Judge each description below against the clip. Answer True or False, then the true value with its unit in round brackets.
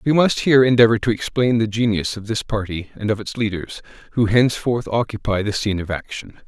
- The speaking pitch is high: False (110 Hz)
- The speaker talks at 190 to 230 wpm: True (205 wpm)